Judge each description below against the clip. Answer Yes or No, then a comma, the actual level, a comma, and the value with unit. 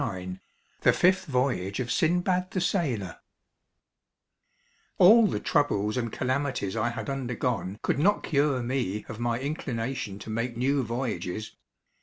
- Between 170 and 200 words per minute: No, slow, 135 wpm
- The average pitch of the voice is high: No, low, 125 Hz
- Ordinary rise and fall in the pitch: Yes, average, 4.8 semitones